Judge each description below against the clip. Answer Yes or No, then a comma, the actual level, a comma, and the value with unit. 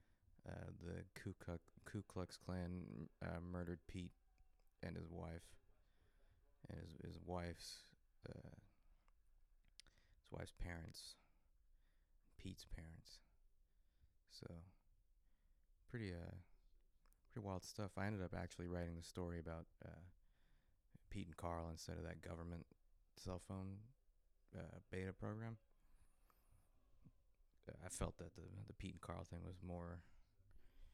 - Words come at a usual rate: No, slow, 120 wpm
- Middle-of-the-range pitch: No, very low, 90 Hz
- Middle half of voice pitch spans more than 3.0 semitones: No, narrow, 2.5 semitones